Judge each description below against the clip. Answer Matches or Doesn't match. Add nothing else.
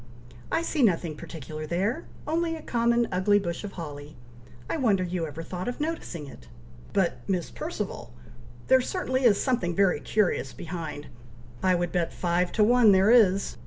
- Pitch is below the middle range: Doesn't match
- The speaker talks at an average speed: Matches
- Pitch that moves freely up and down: Matches